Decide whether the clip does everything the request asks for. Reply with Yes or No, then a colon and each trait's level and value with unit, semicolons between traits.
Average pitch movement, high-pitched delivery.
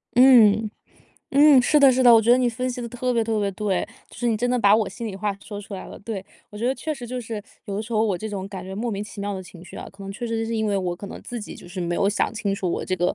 Yes: average, 3.5 semitones; high, 215 Hz